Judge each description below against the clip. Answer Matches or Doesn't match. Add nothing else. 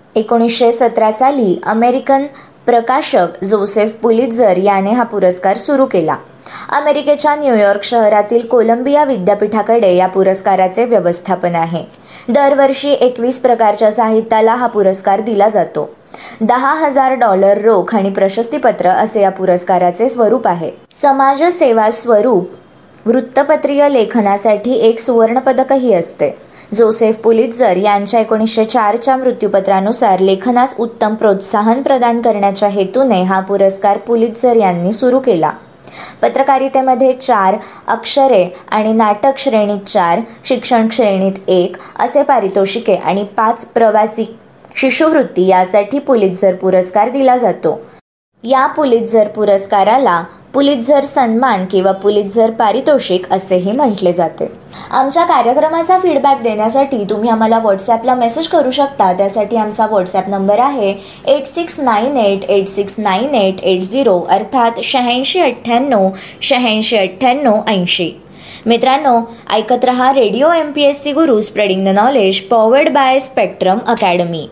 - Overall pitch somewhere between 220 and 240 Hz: Matches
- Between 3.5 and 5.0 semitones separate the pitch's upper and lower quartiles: Matches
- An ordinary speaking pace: Matches